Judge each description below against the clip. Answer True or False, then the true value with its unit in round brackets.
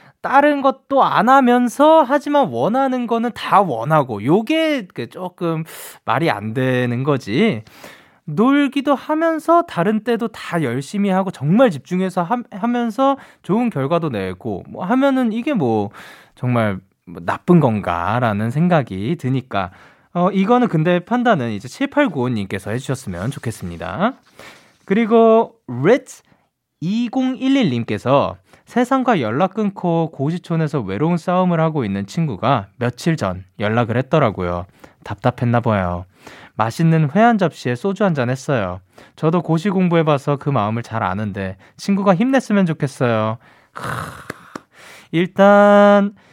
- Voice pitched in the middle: True (165 Hz)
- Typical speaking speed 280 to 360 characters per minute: False (265 characters per minute)